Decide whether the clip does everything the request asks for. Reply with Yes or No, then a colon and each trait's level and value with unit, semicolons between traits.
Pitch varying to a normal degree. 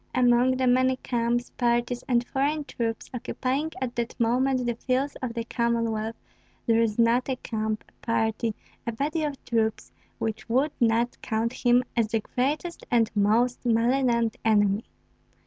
No: narrow, 2.1 semitones